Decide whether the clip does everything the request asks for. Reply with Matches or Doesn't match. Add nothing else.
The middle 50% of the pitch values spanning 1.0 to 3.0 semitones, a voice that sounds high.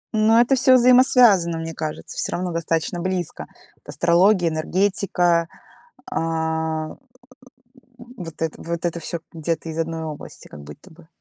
Doesn't match